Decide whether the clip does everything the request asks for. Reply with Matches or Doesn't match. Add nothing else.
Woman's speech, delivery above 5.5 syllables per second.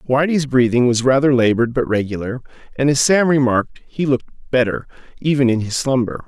Doesn't match